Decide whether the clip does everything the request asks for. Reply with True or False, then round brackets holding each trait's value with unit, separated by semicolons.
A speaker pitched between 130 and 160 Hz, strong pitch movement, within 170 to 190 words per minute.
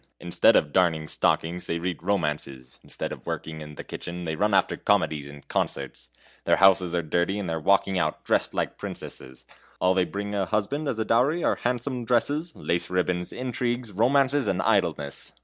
False (90 Hz; 5.8 semitones; 185 wpm)